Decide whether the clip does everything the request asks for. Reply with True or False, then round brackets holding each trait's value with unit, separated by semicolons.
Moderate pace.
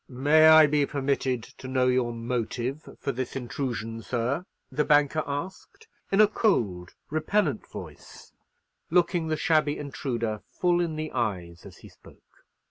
True (145 wpm)